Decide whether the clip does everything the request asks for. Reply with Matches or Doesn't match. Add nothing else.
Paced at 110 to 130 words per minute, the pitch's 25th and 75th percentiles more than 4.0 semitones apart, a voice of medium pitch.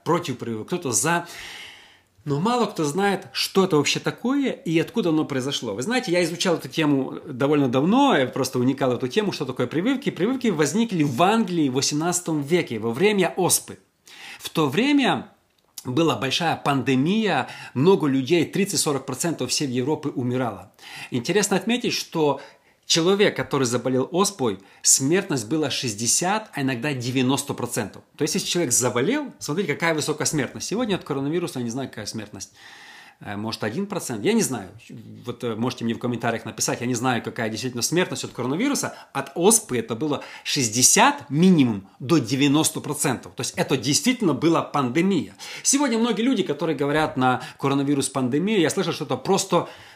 Doesn't match